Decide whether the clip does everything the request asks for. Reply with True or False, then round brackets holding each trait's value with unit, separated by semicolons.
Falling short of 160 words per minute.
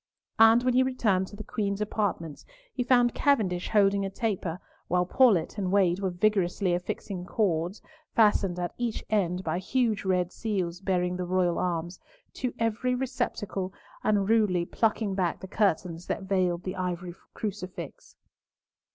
True (150 wpm)